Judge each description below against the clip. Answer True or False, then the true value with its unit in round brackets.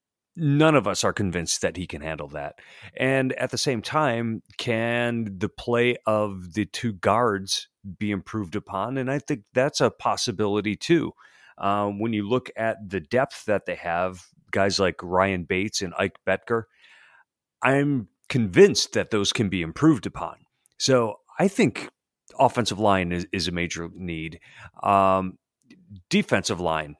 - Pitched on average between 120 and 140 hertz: False (105 Hz)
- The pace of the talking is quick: False (155 wpm)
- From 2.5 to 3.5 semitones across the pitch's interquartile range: False (4.4 semitones)